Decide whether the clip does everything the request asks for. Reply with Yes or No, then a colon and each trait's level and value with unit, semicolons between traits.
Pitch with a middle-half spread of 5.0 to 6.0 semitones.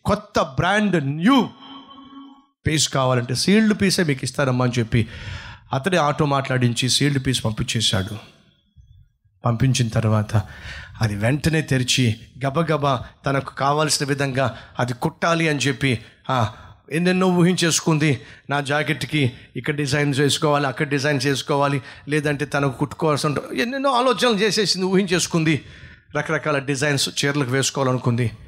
No: average, 4.2 semitones